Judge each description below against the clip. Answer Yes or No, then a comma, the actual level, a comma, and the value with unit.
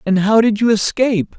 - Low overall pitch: No, high, 215 Hz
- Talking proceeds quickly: Yes, fast, 215 wpm